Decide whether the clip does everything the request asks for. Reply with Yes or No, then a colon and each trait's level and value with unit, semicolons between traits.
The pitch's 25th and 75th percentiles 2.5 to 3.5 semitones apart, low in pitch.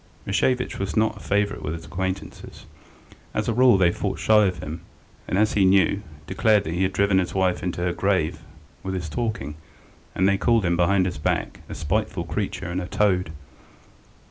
Yes: average, 2.8 semitones; very low, 95 Hz